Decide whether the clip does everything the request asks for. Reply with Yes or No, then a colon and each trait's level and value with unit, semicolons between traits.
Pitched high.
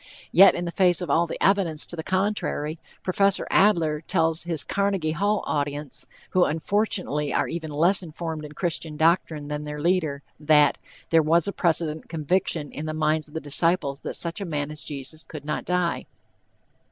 No: medium, 160 Hz